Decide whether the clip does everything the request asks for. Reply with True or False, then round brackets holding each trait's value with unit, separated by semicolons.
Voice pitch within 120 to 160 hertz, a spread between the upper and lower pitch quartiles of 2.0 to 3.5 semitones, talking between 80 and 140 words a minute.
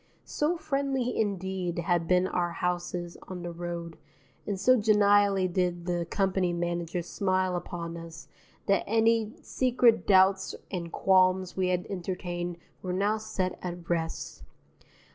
False (185 Hz; 2.6 semitones; 135 wpm)